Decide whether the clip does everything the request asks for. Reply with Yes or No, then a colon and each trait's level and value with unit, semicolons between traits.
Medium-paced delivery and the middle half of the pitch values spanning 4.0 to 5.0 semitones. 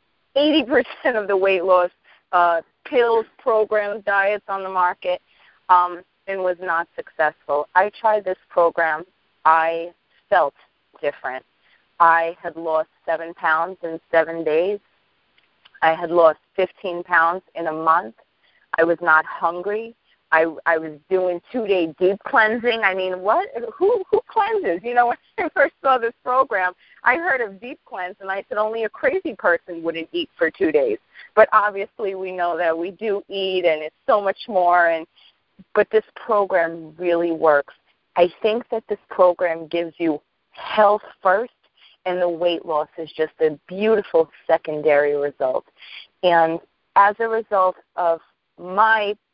Yes: average, 155 wpm; average, 4.4 semitones